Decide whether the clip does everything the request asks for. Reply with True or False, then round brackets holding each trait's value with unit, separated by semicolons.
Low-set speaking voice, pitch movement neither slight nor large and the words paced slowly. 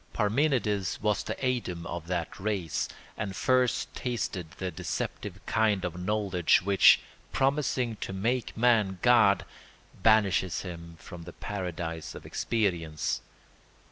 True (100 Hz; 4.3 semitones; 120 wpm)